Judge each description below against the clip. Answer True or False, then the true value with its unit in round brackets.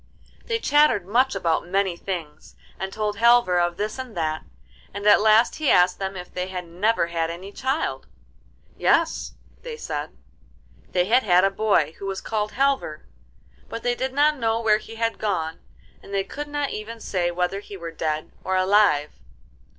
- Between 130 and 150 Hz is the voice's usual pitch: False (200 Hz)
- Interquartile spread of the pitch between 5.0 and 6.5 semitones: False (4.5 semitones)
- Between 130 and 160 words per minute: False (180 wpm)